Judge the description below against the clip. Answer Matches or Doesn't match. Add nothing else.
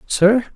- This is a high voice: Matches